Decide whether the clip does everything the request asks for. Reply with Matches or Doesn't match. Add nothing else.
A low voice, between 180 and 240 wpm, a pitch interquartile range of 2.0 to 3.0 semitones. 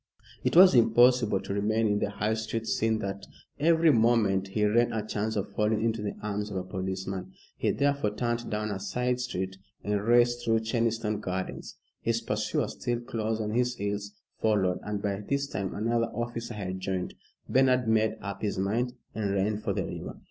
Matches